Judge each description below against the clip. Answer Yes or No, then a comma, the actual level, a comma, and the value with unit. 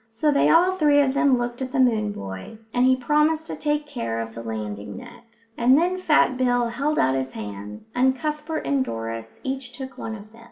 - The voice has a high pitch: Yes, very high, 250 Hz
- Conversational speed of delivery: No, fast, 215 wpm